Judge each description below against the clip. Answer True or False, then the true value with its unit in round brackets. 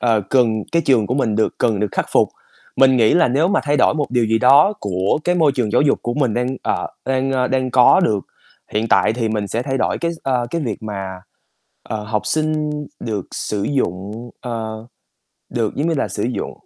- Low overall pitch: True (125 Hz)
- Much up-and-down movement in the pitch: False (4.1 semitones)